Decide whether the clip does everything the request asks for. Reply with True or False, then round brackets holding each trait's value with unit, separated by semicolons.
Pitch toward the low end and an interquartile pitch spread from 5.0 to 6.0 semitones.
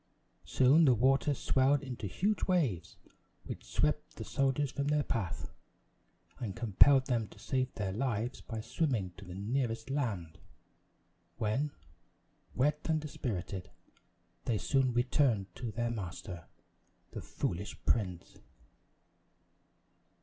True (120 Hz; 5.3 semitones)